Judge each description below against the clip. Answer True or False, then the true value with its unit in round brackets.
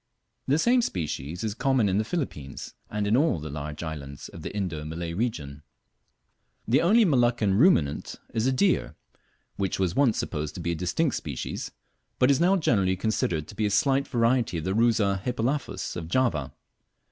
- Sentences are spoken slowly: False (180 wpm)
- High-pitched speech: False (105 Hz)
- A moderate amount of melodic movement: False (7.7 semitones)